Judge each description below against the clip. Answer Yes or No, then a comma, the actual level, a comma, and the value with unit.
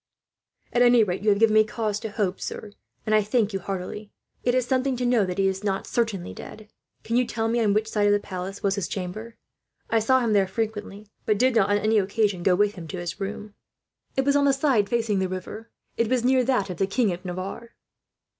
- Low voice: No, high, 210 Hz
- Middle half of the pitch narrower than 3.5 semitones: Yes, average, 3.0 semitones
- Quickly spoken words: Yes, fast, 240 wpm